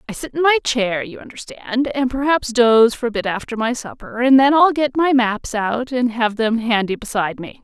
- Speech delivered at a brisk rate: Yes, fast, 230 wpm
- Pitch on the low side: No, high, 240 Hz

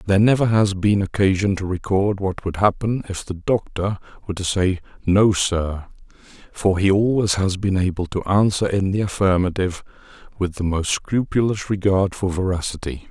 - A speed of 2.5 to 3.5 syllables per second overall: No, 5.1 syllables/s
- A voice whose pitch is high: No, very low, 95 Hz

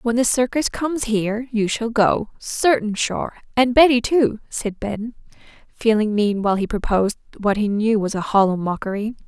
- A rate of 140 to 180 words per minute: Yes, average, 175 wpm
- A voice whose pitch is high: Yes, high, 220 Hz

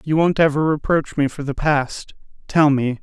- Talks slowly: No, average, 200 wpm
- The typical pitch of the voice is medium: Yes, medium, 150 Hz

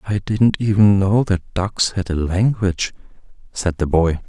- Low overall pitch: Yes, very low, 95 Hz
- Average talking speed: Yes, average, 170 wpm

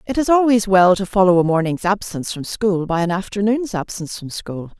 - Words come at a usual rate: No, fast, 215 wpm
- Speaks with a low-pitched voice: No, high, 195 Hz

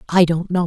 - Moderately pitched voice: Yes, medium, 175 Hz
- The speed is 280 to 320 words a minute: No, fast, 270 wpm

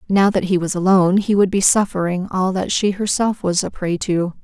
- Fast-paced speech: Yes, fast, 230 wpm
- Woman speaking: Yes, female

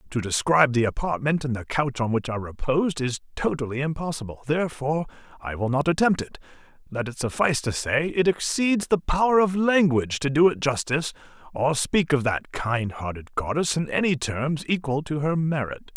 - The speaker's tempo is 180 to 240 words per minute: Yes, average, 185 wpm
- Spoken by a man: Yes, male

